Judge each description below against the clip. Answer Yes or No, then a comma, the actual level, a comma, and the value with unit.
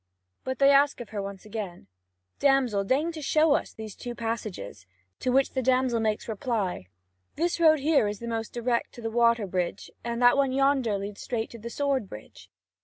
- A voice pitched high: Yes, high, 235 Hz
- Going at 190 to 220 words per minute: Yes, average, 195 wpm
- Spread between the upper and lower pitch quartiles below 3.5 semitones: No, average, 4.5 semitones